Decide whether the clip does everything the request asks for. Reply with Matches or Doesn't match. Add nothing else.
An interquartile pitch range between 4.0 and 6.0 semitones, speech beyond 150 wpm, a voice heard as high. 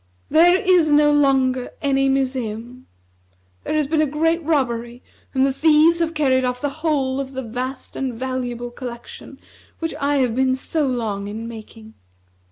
Doesn't match